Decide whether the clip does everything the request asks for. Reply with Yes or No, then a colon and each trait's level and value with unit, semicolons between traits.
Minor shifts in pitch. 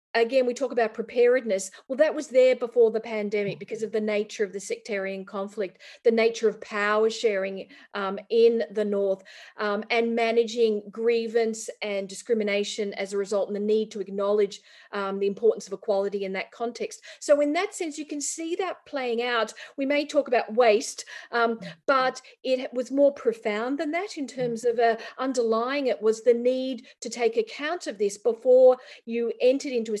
No: average, 3.8 semitones